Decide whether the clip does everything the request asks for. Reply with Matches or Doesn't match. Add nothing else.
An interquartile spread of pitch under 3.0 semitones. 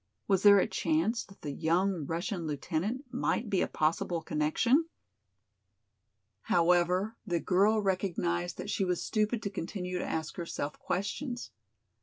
Doesn't match